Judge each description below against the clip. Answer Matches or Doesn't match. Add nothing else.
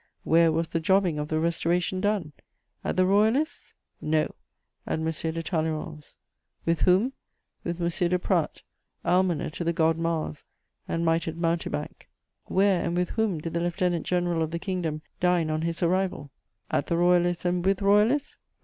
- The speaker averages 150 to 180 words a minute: Matches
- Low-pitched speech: Doesn't match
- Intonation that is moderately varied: Doesn't match